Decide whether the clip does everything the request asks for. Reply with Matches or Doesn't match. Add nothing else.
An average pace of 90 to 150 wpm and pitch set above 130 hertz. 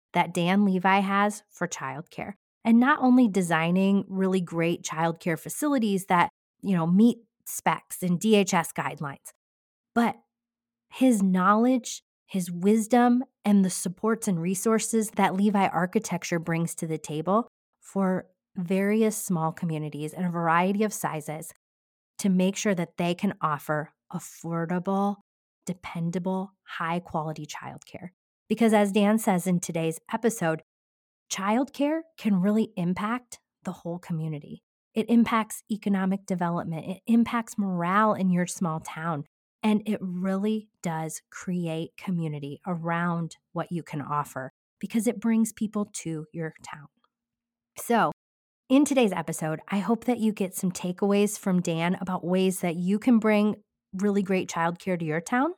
Matches